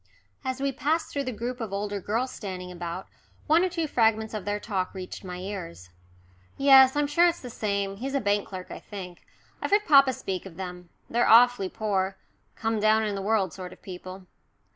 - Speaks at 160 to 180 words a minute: No, fast, 205 wpm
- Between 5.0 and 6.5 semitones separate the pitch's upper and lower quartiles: Yes, wide, 5.4 semitones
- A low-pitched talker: No, high, 210 Hz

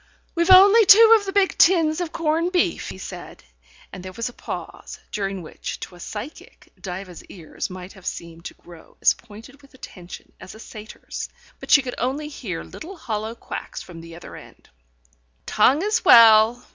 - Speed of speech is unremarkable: Yes, average, 185 wpm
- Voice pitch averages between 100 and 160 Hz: No, high, 230 Hz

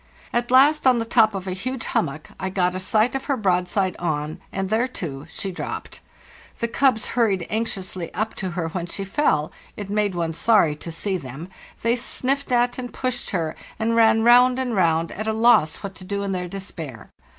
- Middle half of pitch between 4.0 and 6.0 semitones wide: Yes, average, 4.9 semitones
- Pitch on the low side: No, high, 200 Hz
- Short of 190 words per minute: No, average, 195 wpm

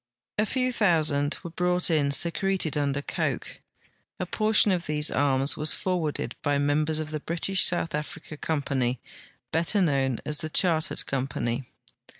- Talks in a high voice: No, medium, 155 Hz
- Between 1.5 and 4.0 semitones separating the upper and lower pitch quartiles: Yes, average, 3.6 semitones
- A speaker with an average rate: Yes, average, 155 wpm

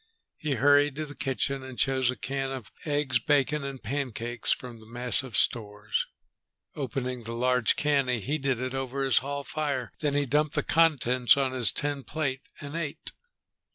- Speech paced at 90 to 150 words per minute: No, average, 175 wpm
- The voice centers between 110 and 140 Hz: Yes, low, 135 Hz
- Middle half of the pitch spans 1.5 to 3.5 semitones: Yes, narrow, 2.5 semitones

